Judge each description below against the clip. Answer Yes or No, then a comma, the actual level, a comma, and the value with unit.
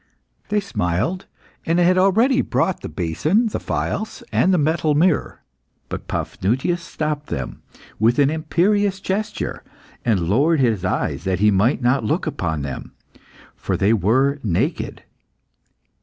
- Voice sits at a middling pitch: Yes, medium, 150 Hz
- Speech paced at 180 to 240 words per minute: No, average, 140 wpm